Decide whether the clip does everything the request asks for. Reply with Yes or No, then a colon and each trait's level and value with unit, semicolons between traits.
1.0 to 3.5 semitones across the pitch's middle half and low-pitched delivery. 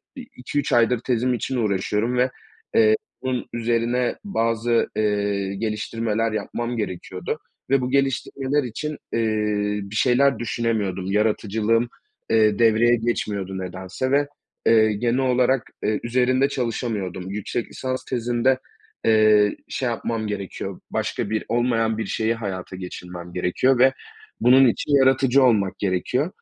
Yes: average, 3.2 semitones; low, 115 Hz